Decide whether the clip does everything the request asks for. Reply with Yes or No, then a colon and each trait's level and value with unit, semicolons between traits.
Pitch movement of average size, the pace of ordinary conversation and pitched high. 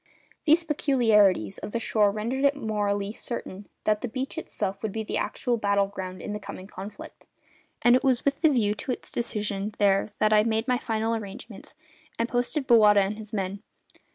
Yes: average, 3.2 semitones; average, 190 wpm; high, 215 Hz